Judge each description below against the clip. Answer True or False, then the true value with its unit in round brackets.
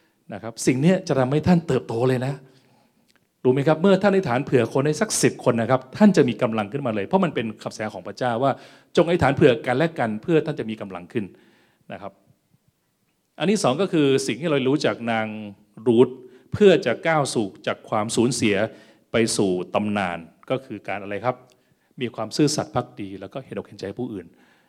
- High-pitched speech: False (125 Hz)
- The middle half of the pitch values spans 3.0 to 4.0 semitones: False (4.6 semitones)